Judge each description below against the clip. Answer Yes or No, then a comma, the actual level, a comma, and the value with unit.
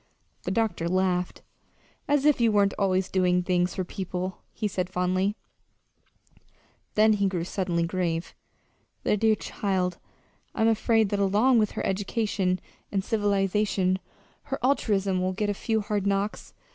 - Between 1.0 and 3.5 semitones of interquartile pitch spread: Yes, narrow, 2.5 semitones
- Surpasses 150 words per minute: No, average, 145 wpm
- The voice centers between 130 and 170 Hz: No, high, 195 Hz